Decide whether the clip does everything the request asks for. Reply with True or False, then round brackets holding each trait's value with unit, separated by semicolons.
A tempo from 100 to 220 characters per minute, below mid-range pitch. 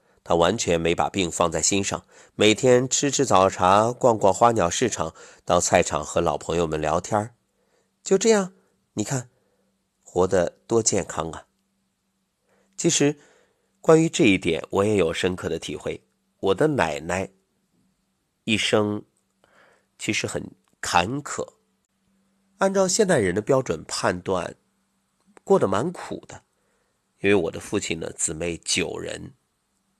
True (190 characters per minute; 115 Hz)